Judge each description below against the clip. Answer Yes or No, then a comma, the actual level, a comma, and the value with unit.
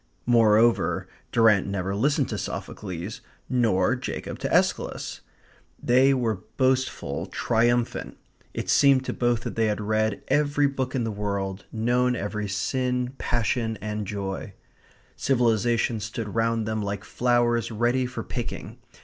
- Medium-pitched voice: No, low, 115 Hz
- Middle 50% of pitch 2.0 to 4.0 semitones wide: Yes, average, 2.9 semitones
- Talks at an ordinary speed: No, slow, 130 wpm